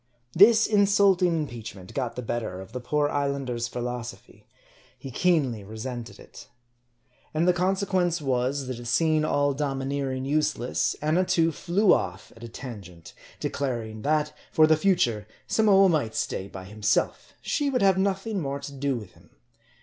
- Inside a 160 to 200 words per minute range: No, average, 150 wpm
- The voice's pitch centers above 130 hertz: Yes, medium, 140 Hz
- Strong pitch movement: Yes, wide, 6.5 semitones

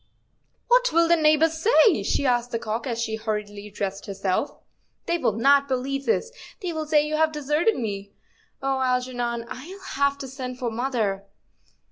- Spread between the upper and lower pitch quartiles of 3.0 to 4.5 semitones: No, average, 5.3 semitones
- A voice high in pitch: Yes, very high, 260 Hz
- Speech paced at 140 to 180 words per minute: Yes, average, 175 wpm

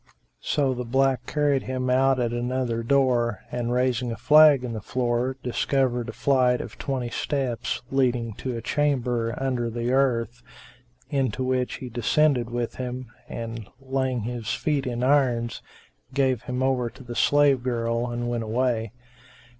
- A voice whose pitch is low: Yes, low, 125 Hz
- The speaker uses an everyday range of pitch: No, narrow, 1.9 semitones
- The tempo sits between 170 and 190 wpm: No, average, 160 wpm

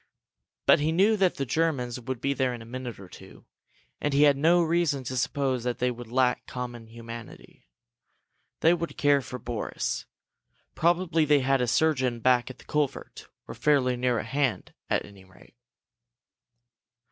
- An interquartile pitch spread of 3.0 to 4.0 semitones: Yes, average, 3.5 semitones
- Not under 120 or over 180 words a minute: Yes, average, 170 wpm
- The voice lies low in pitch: Yes, low, 130 Hz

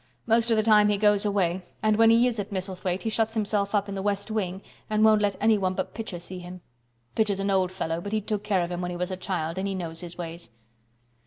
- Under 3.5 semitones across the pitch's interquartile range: Yes, average, 2.8 semitones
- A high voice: Yes, high, 200 Hz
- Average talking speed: No, fast, 260 wpm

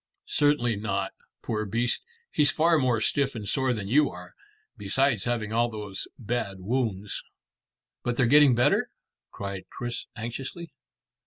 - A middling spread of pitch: Yes, average, 4.2 semitones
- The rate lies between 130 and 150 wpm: Yes, average, 140 wpm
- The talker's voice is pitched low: Yes, low, 120 Hz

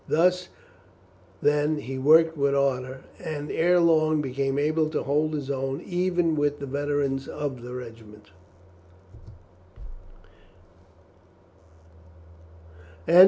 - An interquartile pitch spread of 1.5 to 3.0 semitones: Yes, narrow, 2.6 semitones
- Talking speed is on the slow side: Yes, slow, 100 wpm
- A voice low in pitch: No, medium, 145 Hz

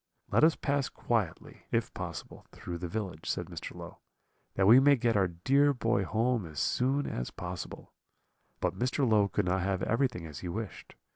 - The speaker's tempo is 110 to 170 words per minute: No, average, 185 wpm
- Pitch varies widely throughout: Yes, wide, 6.1 semitones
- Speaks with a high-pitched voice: No, low, 110 Hz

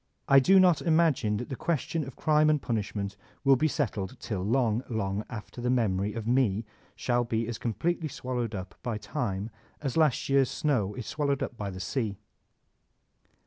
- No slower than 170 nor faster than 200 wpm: Yes, average, 180 wpm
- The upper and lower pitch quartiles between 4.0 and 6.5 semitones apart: Yes, average, 4.8 semitones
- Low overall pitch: Yes, low, 120 Hz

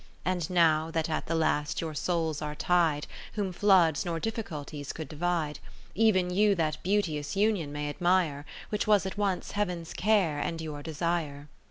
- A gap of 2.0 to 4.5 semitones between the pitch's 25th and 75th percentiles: Yes, average, 3.6 semitones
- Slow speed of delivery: No, average, 165 wpm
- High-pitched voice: No, medium, 165 Hz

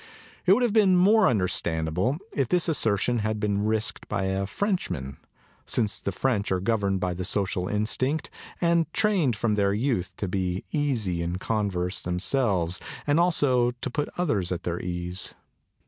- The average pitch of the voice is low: Yes, low, 105 Hz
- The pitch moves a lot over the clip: Yes, wide, 7.0 semitones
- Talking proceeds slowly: No, average, 165 wpm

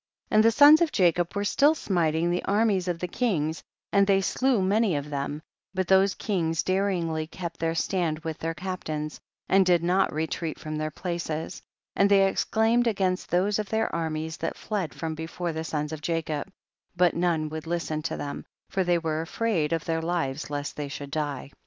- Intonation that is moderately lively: Yes, average, 3.6 semitones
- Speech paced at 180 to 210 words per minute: Yes, average, 200 wpm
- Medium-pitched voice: Yes, medium, 170 Hz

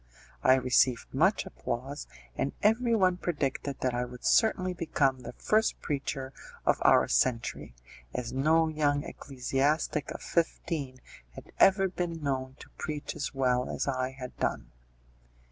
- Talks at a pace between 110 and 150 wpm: Yes, average, 145 wpm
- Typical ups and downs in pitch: Yes, average, 4.2 semitones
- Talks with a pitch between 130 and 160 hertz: Yes, medium, 140 Hz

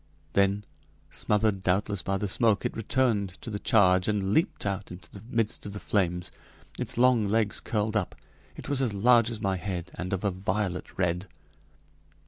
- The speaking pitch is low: Yes, low, 100 Hz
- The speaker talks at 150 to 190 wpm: Yes, average, 180 wpm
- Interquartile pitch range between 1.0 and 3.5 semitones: Yes, average, 2.7 semitones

